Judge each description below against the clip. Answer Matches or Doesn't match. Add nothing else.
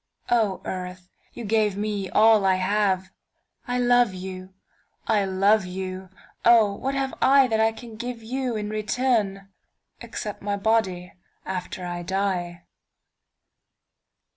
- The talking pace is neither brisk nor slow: Doesn't match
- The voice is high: Matches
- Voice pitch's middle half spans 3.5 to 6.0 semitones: Doesn't match